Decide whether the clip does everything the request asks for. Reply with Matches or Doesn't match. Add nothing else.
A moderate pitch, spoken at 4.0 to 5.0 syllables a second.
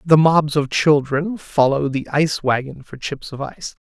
Matches